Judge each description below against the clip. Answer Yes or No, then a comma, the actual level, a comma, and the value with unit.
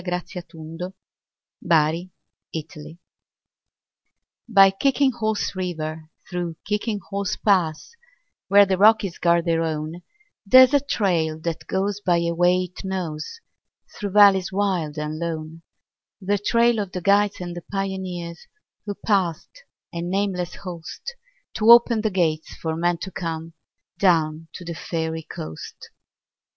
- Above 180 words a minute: No, slow, 135 wpm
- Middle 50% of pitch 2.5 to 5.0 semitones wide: Yes, average, 3.5 semitones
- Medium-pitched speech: Yes, medium, 180 Hz